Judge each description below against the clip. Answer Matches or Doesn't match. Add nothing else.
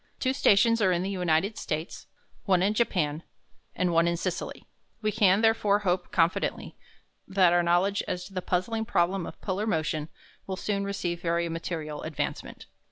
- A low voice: Doesn't match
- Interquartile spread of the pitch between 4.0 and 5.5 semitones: Doesn't match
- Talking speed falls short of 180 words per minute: Matches